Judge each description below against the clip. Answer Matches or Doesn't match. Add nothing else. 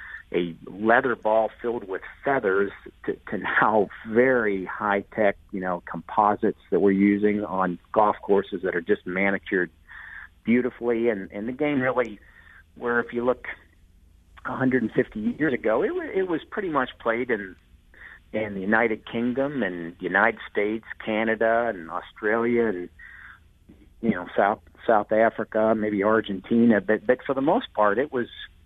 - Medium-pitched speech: Doesn't match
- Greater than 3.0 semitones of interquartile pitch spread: Matches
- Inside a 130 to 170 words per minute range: Matches